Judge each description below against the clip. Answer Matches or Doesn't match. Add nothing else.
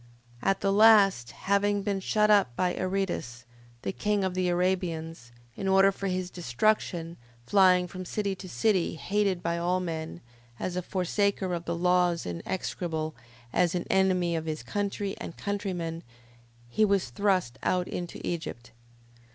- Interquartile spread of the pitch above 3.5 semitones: Doesn't match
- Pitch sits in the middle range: Matches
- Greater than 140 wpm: Matches